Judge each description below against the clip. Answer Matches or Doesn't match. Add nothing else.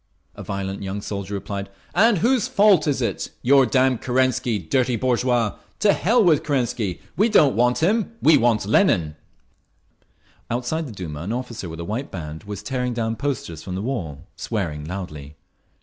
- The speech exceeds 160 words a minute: Matches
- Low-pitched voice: Matches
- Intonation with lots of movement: Matches